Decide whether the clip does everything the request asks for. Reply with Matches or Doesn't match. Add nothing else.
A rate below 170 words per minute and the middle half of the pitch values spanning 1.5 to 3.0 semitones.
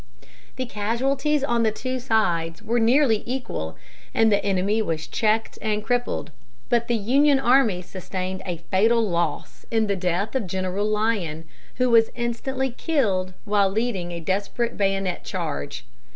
Doesn't match